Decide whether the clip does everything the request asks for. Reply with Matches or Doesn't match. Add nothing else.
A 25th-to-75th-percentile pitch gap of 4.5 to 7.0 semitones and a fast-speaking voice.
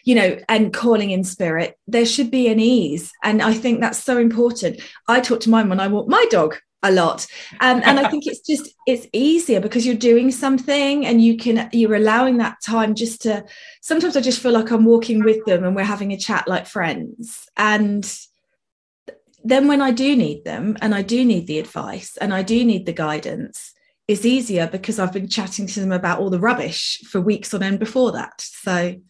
Doesn't match